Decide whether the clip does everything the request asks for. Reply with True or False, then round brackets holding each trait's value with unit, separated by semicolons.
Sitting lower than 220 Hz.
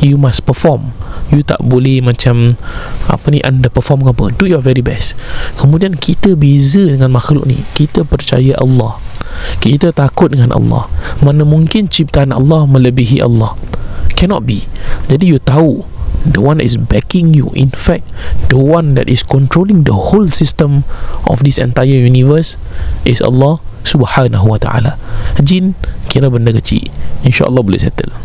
True (135 Hz)